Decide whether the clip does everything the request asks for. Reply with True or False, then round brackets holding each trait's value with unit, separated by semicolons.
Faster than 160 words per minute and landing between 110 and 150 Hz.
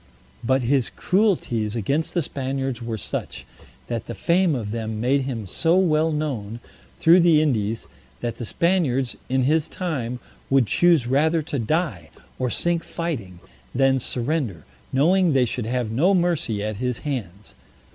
False (155 wpm; 135 Hz)